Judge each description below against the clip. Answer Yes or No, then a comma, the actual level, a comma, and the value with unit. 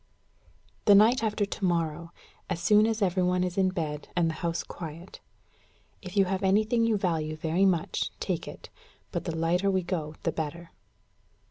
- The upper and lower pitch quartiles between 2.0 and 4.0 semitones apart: Yes, average, 3.1 semitones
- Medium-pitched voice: Yes, medium, 180 Hz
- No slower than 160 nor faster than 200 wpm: Yes, average, 175 wpm